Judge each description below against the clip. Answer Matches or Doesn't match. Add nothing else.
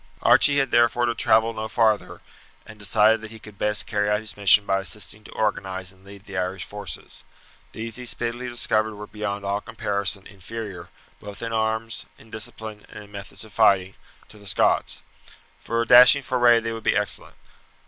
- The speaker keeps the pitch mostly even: Matches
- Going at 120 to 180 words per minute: Doesn't match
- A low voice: Matches